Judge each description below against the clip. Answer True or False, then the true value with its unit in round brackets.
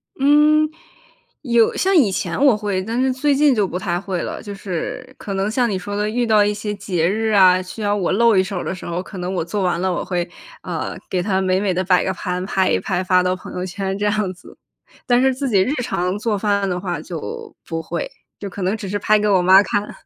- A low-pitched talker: False (200 Hz)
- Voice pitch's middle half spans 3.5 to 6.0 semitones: False (2.9 semitones)